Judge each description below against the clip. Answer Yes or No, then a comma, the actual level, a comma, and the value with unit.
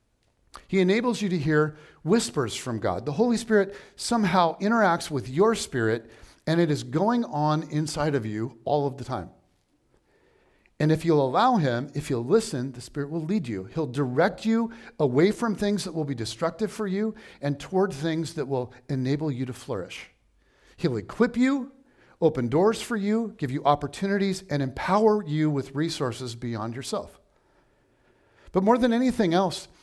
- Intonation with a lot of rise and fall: Yes, wide, 7.4 semitones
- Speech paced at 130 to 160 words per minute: No, average, 170 wpm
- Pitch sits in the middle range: Yes, medium, 155 Hz